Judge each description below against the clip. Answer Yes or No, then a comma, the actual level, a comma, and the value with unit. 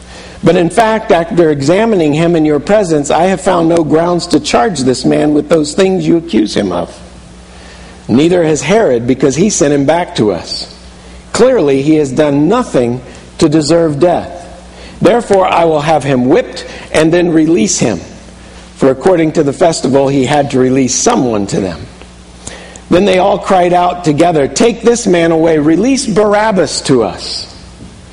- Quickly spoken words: No, average, 170 wpm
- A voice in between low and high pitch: Yes, medium, 155 Hz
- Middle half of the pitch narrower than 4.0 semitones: No, wide, 5.5 semitones